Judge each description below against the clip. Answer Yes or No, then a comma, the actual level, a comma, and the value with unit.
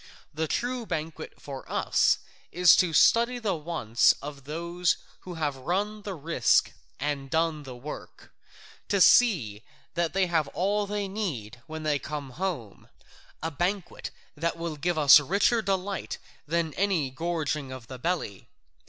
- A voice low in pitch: No, medium, 165 Hz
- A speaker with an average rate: Yes, average, 150 wpm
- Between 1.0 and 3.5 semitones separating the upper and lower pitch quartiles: No, average, 4.8 semitones